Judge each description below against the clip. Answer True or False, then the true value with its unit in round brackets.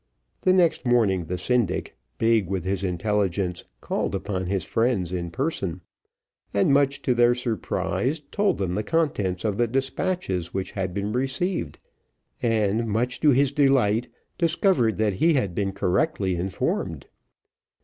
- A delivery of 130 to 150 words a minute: True (145 wpm)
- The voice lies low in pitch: True (110 Hz)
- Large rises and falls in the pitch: True (5.9 semitones)